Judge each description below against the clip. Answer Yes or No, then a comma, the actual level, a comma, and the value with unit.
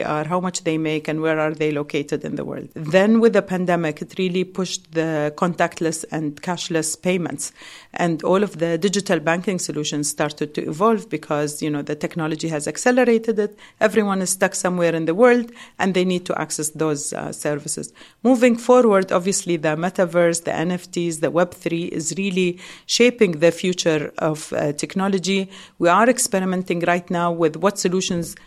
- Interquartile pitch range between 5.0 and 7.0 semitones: No, average, 3.4 semitones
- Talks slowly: No, average, 175 wpm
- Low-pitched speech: No, medium, 175 Hz